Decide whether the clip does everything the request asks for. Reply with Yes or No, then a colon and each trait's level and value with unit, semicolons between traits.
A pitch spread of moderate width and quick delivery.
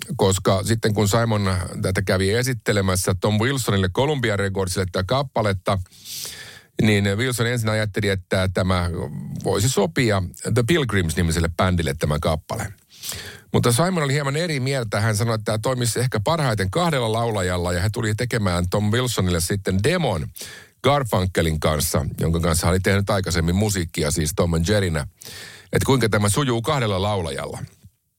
No: average, 4.2 semitones; average, 145 wpm